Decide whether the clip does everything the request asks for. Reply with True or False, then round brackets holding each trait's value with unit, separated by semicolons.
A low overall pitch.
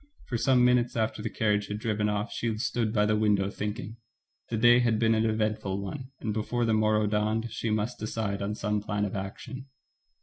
True (110 Hz)